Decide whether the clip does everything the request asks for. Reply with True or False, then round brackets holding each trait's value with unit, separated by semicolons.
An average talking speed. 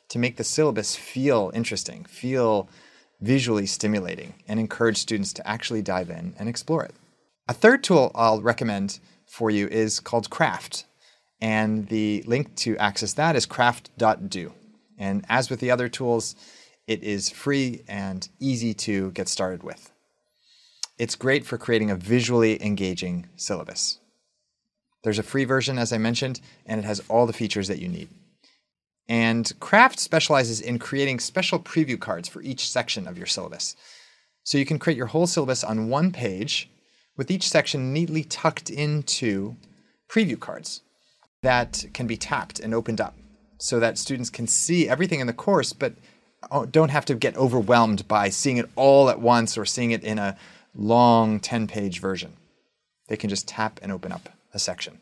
True (170 wpm)